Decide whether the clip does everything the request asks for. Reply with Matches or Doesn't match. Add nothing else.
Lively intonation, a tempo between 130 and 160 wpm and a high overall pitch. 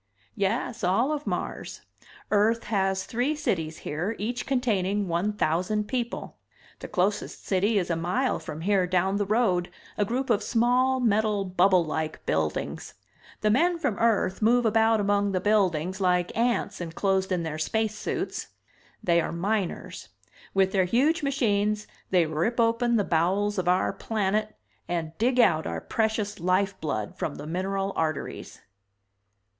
Doesn't match